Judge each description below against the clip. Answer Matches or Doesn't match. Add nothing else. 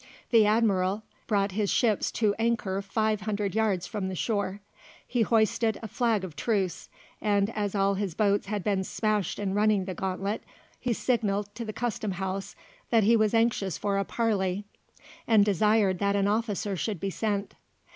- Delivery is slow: Doesn't match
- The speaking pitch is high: Matches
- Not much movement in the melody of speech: Matches